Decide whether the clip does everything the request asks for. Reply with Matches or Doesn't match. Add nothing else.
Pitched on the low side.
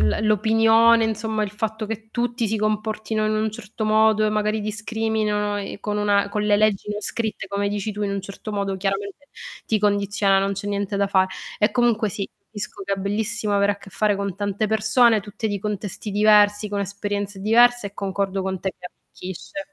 Doesn't match